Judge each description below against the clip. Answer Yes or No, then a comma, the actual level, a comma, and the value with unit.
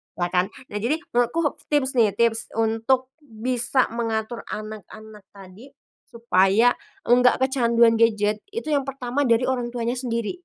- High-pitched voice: Yes, high, 235 Hz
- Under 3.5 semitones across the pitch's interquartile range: Yes, average, 2.9 semitones